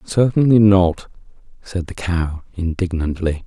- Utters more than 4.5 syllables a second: No, 3.9 syllables/s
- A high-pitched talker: No, very low, 90 Hz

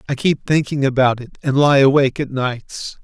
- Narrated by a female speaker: No, male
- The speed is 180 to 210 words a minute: Yes, average, 200 wpm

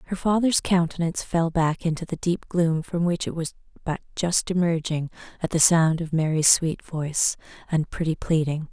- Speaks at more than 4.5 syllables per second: Yes, 5.0 syllables/s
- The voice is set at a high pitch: No, medium, 165 Hz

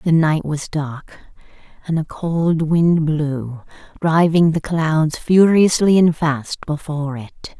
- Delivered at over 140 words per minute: No, slow, 135 wpm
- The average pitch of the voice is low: No, medium, 160 Hz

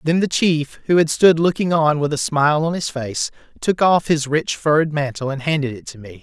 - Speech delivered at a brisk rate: Yes, fast, 240 wpm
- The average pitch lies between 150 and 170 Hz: Yes, medium, 155 Hz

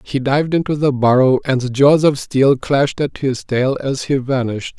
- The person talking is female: No, male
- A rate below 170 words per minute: No, average, 200 wpm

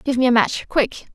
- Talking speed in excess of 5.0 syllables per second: Yes, 5.2 syllables/s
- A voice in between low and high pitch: No, very high, 250 Hz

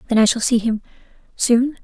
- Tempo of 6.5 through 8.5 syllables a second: No, 5.6 syllables/s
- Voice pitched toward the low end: No, high, 235 Hz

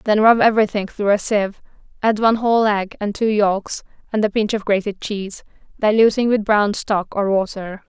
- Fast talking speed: No, average, 190 wpm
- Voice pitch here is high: Yes, high, 210 Hz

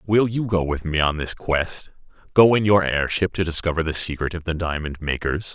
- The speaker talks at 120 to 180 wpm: No, fast, 205 wpm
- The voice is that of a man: Yes, male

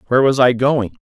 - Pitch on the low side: Yes, low, 125 Hz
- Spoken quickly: Yes, fast, 235 wpm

